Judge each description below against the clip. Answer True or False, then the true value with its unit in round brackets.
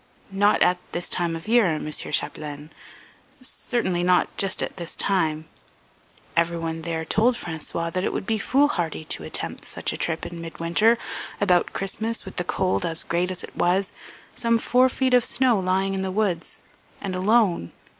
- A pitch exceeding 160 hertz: True (185 Hz)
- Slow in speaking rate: False (170 wpm)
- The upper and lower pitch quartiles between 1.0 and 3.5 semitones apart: False (4.2 semitones)